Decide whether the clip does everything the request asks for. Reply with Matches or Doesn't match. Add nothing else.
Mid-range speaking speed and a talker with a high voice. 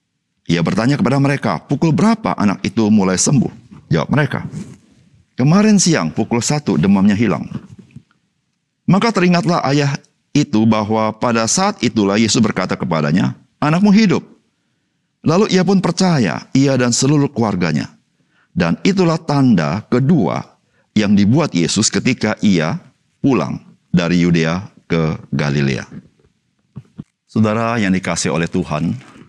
Doesn't match